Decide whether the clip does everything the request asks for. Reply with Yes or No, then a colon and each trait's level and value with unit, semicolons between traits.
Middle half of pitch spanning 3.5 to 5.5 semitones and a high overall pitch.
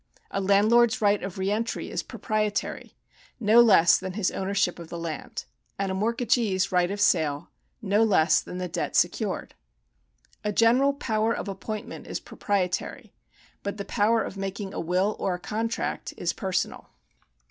No: narrow, 2.6 semitones; high, 200 Hz